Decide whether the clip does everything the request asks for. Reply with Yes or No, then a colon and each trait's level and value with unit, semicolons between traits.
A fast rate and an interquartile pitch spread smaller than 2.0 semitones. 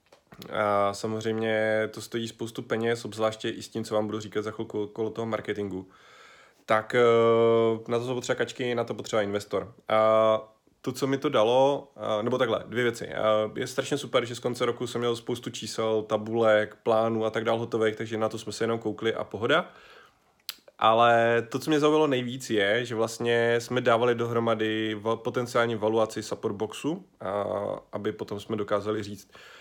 Yes: fast, 175 wpm; narrow, 1.5 semitones